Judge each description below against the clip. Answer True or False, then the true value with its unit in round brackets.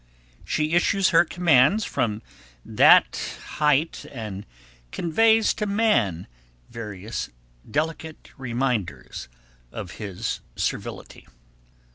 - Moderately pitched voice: True (145 Hz)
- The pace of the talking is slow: True (85 wpm)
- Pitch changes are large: True (8.1 semitones)